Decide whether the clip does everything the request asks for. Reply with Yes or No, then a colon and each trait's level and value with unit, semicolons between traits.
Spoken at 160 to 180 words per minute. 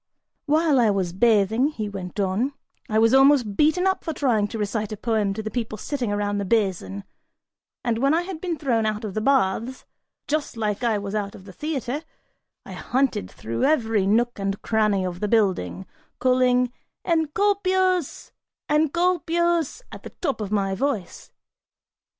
Yes: average, 170 wpm